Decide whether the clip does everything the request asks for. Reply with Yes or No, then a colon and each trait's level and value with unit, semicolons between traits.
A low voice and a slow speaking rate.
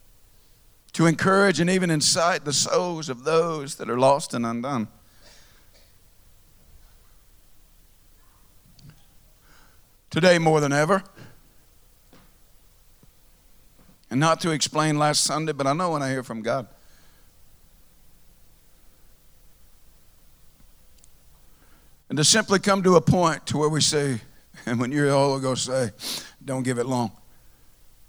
Yes: low, 120 Hz; slow, 115 wpm